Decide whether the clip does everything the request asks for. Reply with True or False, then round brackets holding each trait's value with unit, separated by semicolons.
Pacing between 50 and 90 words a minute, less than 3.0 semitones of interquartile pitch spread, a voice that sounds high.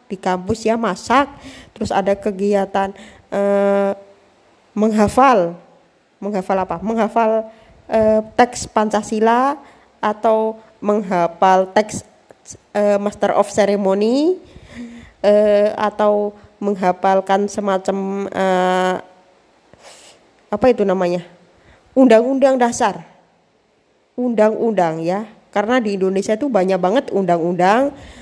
True (85 wpm; 2.5 semitones; 205 Hz)